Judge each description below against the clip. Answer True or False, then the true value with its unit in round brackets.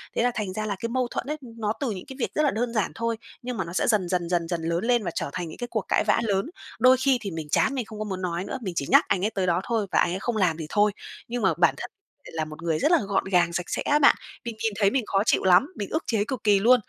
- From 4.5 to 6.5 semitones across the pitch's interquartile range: True (5.0 semitones)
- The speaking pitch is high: True (210 Hz)